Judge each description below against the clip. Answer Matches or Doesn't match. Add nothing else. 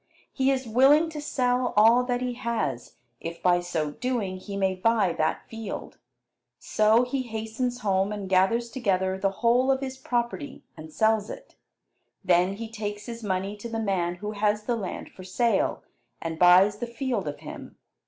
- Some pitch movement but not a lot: Matches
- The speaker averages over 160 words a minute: Matches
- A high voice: Matches